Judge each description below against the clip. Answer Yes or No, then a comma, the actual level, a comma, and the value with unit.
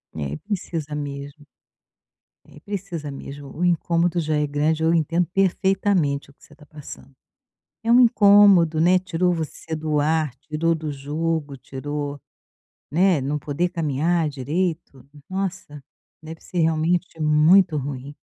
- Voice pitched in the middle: Yes, medium, 160 Hz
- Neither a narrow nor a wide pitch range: Yes, average, 3.3 semitones